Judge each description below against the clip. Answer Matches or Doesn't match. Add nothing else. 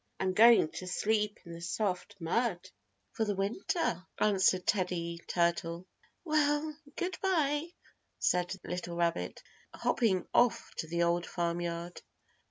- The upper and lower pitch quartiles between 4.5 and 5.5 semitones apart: Matches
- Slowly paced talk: Matches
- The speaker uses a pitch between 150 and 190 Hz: Matches